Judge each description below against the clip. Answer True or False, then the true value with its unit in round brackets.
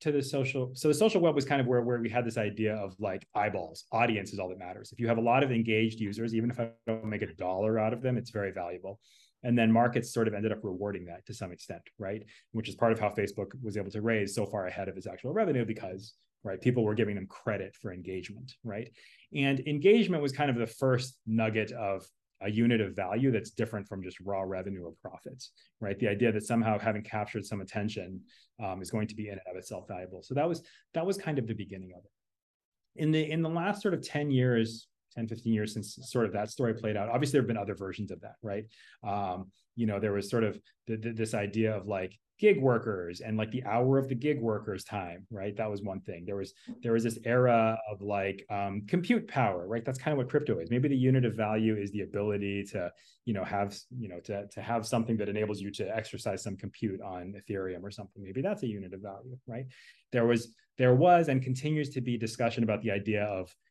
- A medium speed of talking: False (245 wpm)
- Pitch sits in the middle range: False (110 Hz)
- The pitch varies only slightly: False (3.5 semitones)